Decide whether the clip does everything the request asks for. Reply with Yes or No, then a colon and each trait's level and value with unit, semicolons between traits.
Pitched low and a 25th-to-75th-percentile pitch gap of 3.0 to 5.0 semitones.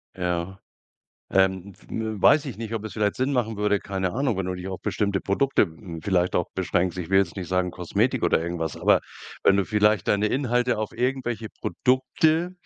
Yes: low, 100 Hz; average, 4.4 semitones